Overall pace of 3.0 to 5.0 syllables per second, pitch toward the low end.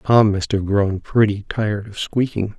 Yes: 4.6 syllables/s; low, 105 Hz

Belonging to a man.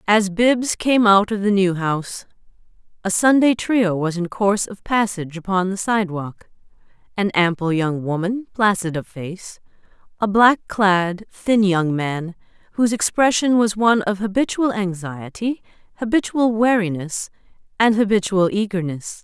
No: female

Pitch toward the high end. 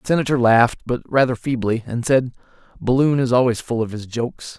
No: low, 125 Hz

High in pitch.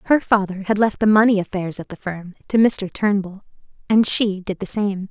Yes: high, 200 Hz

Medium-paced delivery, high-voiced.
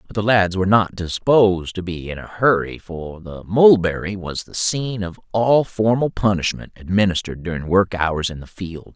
No: average, 190 wpm; very low, 95 Hz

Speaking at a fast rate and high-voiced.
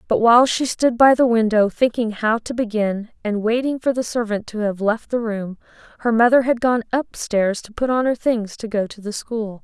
Yes: fast, 230 wpm; high, 225 Hz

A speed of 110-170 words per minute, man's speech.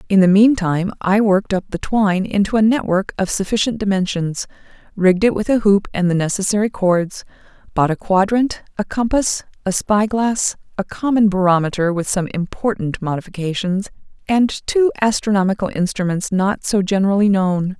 No: average, 160 wpm; female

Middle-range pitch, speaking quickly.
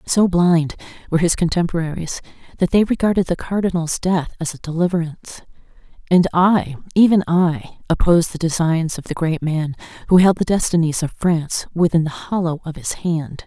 No: medium, 170 Hz; average, 165 wpm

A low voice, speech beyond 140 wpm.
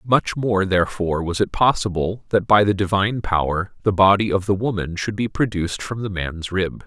Yes: low, 100 Hz; average, 200 wpm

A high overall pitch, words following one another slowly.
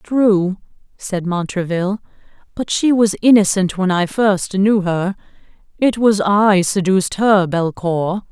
Yes: high, 195 Hz; slow, 130 wpm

